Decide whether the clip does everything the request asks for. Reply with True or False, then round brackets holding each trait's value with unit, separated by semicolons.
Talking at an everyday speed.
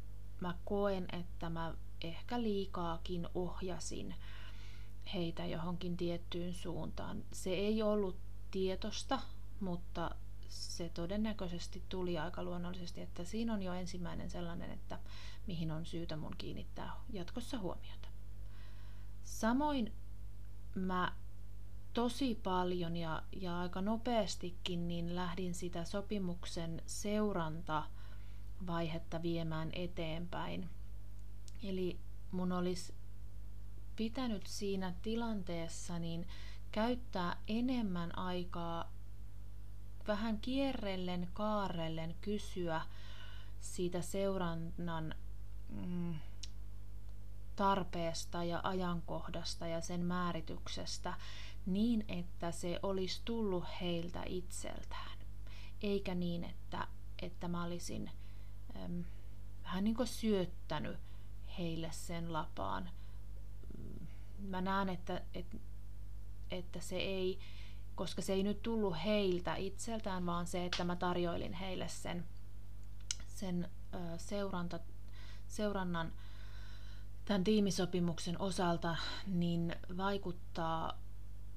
False (90 wpm)